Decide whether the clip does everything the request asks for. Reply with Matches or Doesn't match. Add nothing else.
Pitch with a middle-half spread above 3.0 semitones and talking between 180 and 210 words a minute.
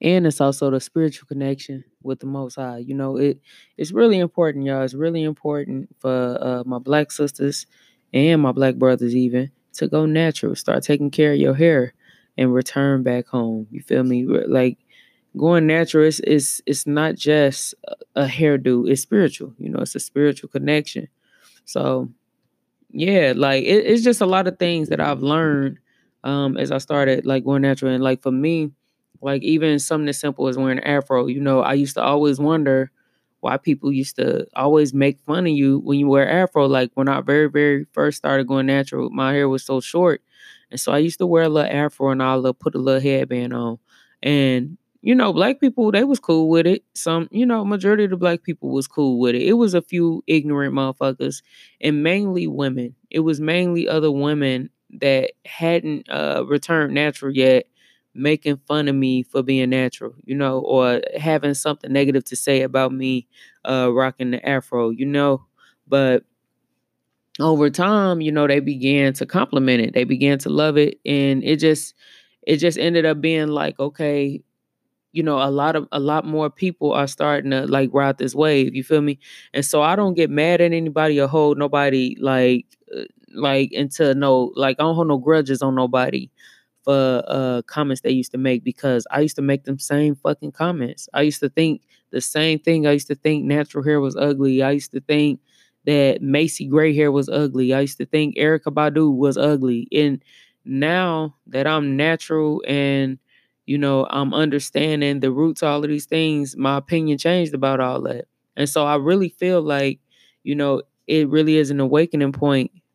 Doesn't match